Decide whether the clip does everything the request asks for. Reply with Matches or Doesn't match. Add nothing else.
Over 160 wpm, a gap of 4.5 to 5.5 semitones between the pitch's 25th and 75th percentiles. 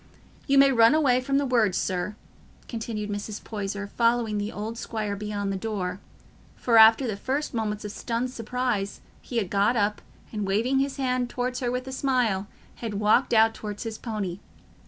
Doesn't match